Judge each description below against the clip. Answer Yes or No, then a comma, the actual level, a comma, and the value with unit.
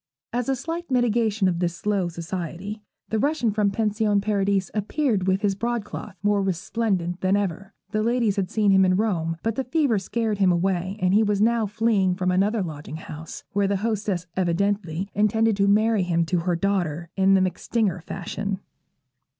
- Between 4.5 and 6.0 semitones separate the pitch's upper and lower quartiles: No, average, 3.0 semitones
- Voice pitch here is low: No, high, 200 Hz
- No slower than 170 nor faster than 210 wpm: Yes, average, 180 wpm